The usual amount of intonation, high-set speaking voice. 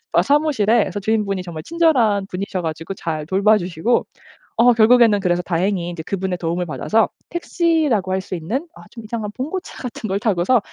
Yes: average, 4.9 semitones; high, 205 Hz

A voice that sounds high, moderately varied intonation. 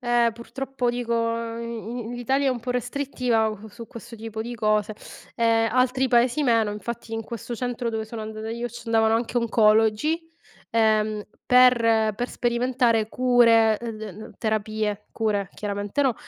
No: high, 230 Hz; narrow, 2.0 semitones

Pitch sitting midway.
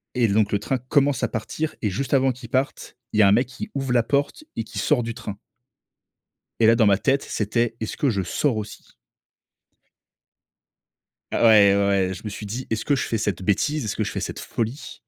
No: low, 115 Hz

